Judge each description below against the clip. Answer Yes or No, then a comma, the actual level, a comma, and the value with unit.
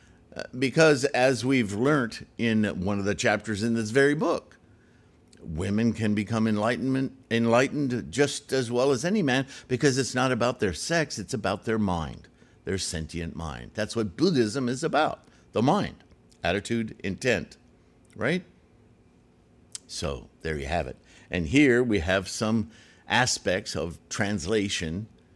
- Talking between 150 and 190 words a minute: No, average, 140 wpm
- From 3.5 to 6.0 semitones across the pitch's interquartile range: Yes, average, 4.7 semitones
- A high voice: No, low, 115 Hz